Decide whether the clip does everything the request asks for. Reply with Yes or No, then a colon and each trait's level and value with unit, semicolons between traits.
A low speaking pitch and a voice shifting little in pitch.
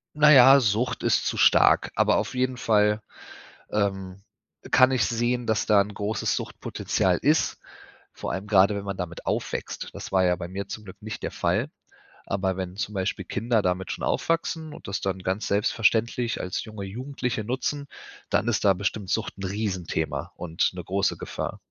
No: low, 105 Hz; average, 3.7 semitones